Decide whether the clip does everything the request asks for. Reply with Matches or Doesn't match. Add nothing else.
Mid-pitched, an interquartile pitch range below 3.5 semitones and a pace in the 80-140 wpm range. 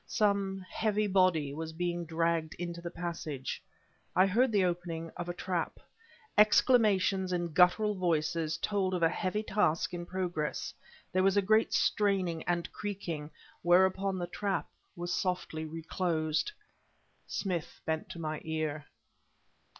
Matches